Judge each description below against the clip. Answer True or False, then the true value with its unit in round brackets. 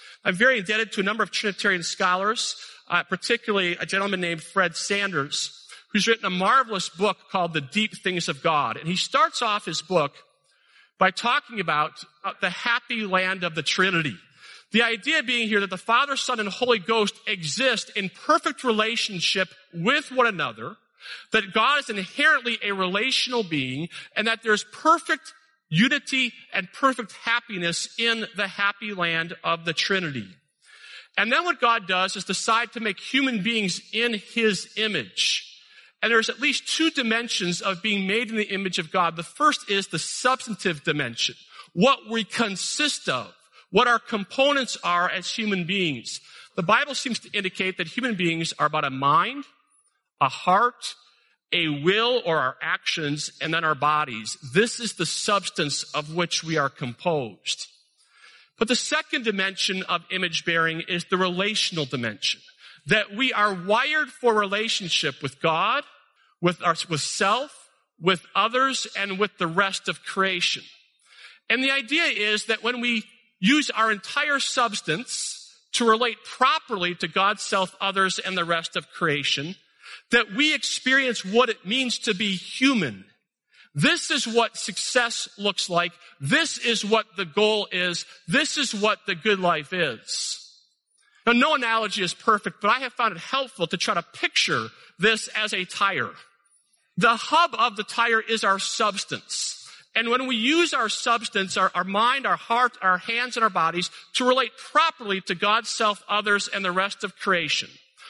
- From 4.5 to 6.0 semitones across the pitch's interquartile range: True (4.8 semitones)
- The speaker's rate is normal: True (165 wpm)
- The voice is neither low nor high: False (210 Hz)